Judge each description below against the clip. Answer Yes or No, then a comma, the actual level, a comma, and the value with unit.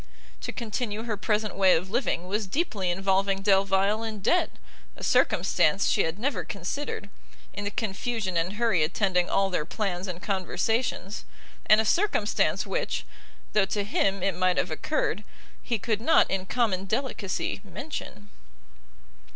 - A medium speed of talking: Yes, average, 150 wpm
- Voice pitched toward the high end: Yes, high, 200 Hz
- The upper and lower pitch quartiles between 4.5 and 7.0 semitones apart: No, average, 3.0 semitones